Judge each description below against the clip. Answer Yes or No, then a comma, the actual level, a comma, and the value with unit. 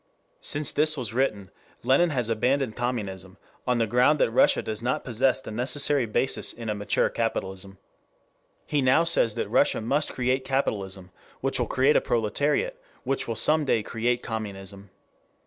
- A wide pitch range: No, average, 4.1 semitones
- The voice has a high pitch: No, low, 120 Hz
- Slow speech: No, average, 165 wpm